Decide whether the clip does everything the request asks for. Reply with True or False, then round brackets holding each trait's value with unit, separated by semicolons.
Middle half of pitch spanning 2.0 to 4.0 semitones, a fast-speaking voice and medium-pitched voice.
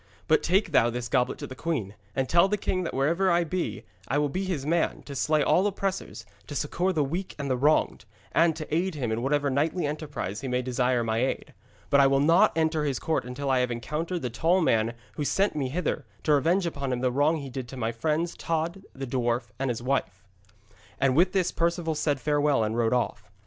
False (4.8 semitones; 230 wpm; 145 Hz)